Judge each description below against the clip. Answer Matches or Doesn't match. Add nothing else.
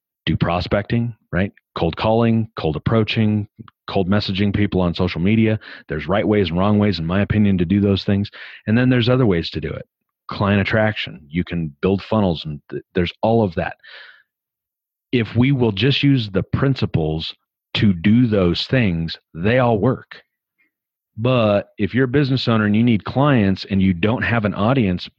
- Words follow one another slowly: Doesn't match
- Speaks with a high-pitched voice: Doesn't match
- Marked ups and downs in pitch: Doesn't match